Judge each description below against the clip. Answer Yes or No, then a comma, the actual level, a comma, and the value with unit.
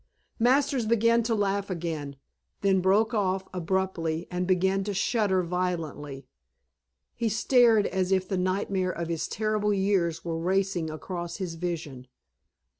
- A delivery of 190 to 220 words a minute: No, slow, 135 wpm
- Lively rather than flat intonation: No, average, 3.3 semitones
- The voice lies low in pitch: No, high, 190 Hz